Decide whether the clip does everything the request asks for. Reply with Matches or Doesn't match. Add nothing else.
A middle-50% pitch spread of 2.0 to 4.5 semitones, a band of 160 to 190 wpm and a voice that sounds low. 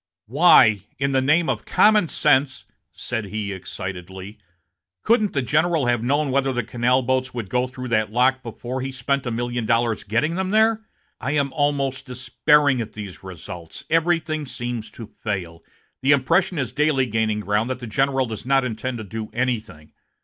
Matches